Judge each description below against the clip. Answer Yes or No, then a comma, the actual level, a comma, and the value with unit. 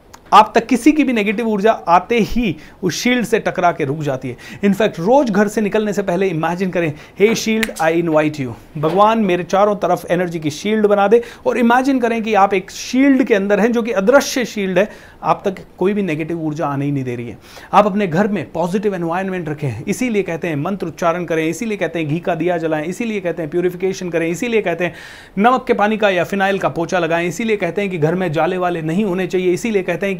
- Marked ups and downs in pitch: No, average, 4.3 semitones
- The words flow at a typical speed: No, fast, 235 wpm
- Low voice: No, high, 190 Hz